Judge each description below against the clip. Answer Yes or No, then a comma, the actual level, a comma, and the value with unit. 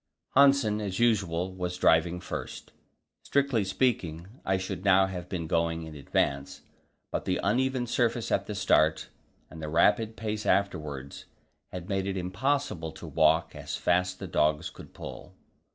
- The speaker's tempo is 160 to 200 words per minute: No, average, 150 wpm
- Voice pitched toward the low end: Yes, very low, 95 Hz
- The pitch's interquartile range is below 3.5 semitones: No, average, 4.7 semitones